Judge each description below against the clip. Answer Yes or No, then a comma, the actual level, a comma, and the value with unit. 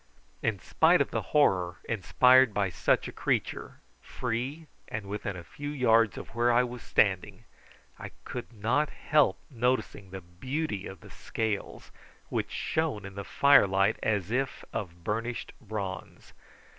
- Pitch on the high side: No, low, 110 Hz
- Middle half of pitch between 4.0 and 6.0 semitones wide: Yes, average, 4.5 semitones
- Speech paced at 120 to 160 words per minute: Yes, average, 150 wpm